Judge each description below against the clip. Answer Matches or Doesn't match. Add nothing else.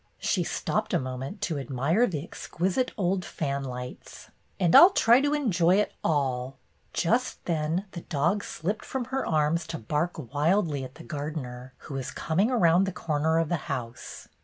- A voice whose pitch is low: Doesn't match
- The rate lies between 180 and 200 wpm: Matches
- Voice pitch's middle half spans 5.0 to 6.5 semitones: Matches